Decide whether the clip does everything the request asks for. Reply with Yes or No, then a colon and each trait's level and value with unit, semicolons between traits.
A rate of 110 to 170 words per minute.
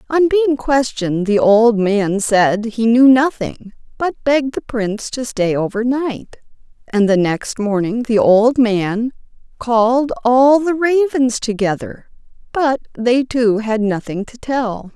Yes: average, 145 wpm